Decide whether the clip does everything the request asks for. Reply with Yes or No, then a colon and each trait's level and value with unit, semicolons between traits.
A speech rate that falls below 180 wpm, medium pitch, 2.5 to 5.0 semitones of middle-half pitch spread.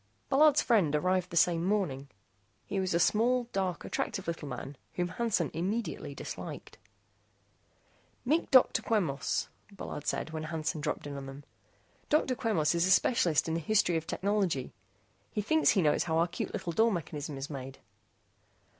No: average, 165 wpm; medium, 175 Hz; wide, 5.6 semitones